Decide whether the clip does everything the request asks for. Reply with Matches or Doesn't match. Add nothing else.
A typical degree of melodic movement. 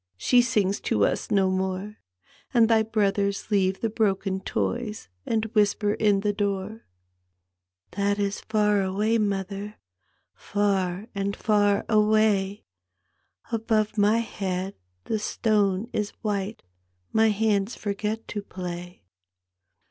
Doesn't match